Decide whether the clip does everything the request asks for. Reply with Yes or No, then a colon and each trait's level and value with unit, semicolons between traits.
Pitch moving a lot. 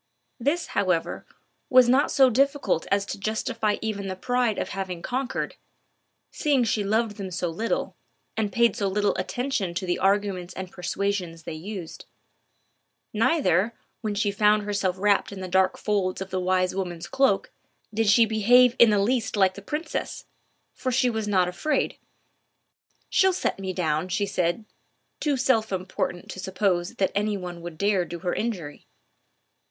No: average, 3.7 semitones